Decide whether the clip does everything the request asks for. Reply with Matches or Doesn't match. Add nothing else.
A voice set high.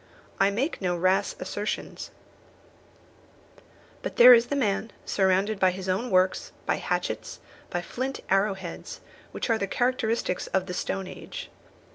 Matches